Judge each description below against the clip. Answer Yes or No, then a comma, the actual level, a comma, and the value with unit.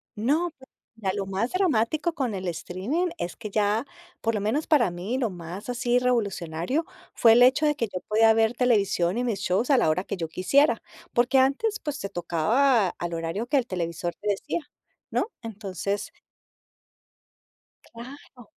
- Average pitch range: No, wide, 5.7 semitones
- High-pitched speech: Yes, high, 225 Hz